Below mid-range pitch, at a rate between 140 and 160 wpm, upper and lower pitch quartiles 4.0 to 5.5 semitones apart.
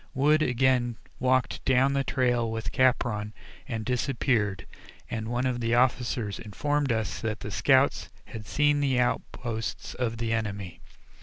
No: low, 120 Hz; average, 145 wpm; average, 2.8 semitones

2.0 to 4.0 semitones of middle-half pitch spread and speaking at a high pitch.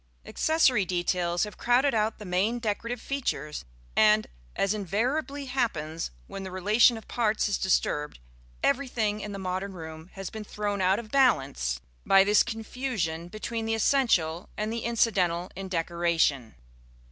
No: average, 4.9 semitones; high, 205 Hz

